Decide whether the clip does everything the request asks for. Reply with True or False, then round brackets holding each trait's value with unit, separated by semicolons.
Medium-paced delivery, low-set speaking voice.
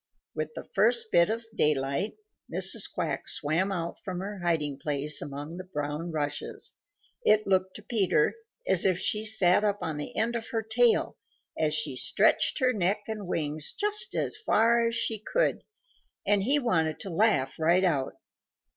False (170 wpm; 185 Hz)